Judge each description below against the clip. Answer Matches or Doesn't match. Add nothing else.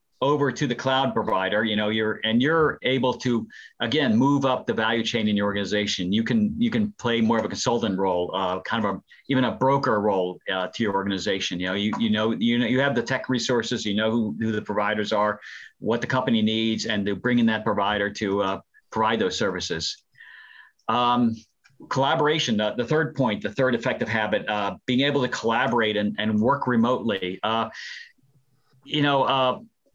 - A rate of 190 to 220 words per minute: Matches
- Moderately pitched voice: Doesn't match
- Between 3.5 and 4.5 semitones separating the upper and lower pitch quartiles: Matches